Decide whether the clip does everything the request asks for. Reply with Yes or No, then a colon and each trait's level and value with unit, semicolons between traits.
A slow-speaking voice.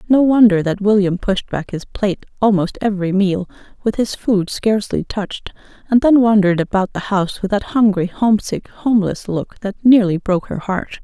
No: average, 180 wpm